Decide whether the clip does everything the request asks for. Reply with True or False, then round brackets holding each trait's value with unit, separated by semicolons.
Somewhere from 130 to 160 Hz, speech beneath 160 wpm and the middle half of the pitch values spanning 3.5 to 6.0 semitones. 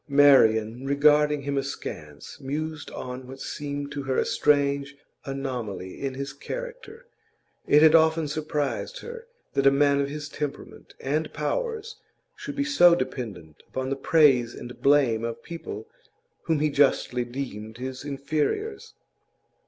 False (140 Hz; 140 wpm; 2.9 semitones)